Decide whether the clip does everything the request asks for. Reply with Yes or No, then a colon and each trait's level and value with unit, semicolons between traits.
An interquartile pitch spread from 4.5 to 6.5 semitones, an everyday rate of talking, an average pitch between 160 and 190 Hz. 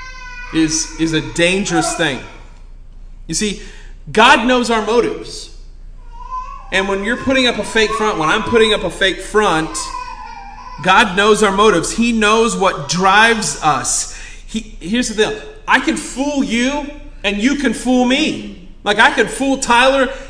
No: wide, 5.5 semitones; average, 155 wpm; high, 230 Hz